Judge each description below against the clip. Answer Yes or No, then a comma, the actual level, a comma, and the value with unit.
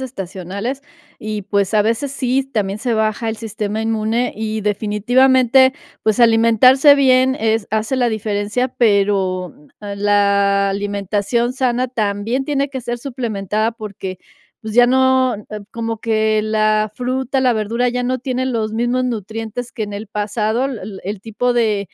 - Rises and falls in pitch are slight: No, average, 3.2 semitones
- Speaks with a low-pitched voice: No, high, 220 Hz